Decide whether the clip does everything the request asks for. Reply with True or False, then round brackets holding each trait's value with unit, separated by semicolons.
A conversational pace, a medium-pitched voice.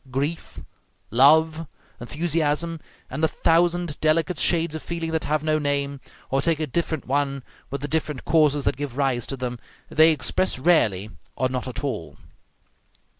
True (160 wpm; 150 Hz)